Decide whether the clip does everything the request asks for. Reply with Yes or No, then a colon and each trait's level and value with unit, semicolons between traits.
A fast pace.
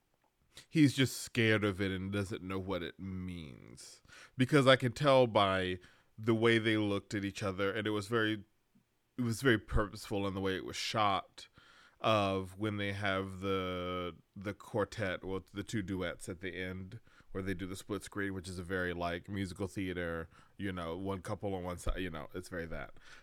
No: average, 195 wpm